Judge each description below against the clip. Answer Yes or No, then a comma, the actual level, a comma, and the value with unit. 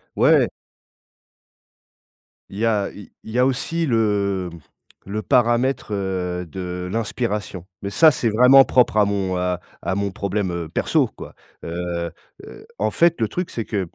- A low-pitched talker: Yes, low, 100 Hz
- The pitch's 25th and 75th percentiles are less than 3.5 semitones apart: No, average, 4.4 semitones